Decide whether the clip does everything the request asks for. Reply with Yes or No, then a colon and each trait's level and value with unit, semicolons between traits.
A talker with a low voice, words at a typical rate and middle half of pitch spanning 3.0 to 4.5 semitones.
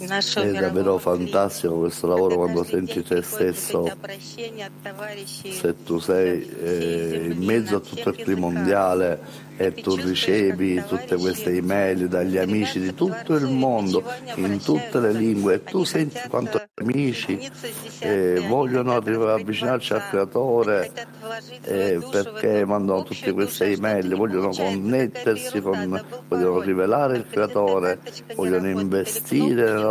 Yes: very low, 95 Hz; average, 125 wpm; average, 4.2 semitones